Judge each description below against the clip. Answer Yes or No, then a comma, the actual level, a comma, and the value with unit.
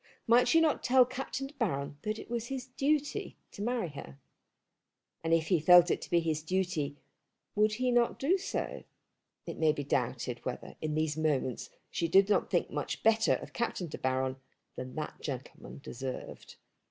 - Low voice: No, medium, 175 Hz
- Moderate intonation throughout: No, wide, 8.6 semitones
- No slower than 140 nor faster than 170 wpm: No, average, 180 wpm